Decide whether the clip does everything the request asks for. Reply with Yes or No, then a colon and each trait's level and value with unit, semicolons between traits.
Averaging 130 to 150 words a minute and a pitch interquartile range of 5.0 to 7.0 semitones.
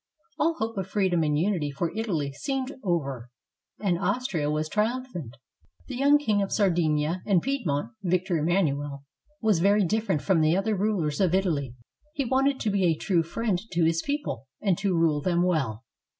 No: average, 175 wpm; wide, 5.5 semitones